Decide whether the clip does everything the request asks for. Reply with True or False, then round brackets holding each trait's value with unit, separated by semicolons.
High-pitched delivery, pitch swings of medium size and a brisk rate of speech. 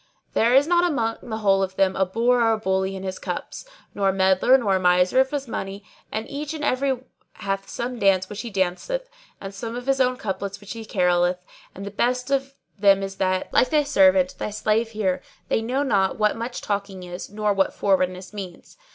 True (210 Hz; 4.6 semitones; 215 wpm)